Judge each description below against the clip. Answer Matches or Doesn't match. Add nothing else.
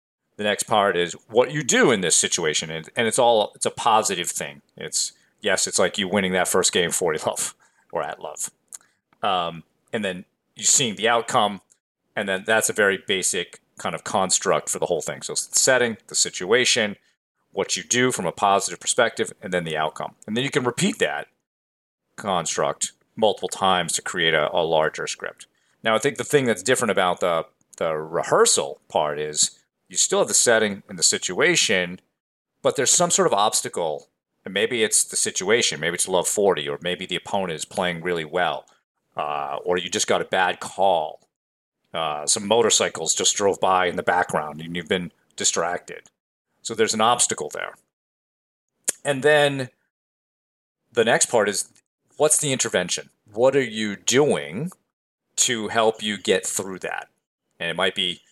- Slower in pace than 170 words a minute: Doesn't match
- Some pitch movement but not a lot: Doesn't match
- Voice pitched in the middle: Doesn't match